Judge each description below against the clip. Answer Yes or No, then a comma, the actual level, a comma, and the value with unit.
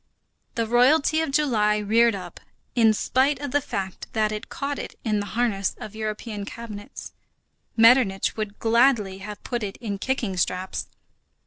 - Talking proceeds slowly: No, average, 155 wpm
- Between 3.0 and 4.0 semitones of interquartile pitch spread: Yes, average, 3.4 semitones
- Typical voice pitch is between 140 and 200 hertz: No, high, 220 Hz